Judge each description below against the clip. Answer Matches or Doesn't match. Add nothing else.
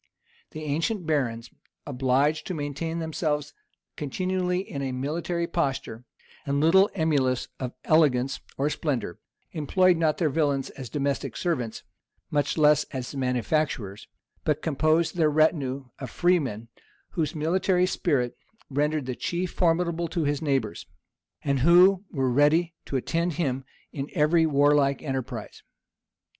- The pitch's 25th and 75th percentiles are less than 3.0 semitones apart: Doesn't match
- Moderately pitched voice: Matches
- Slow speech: Matches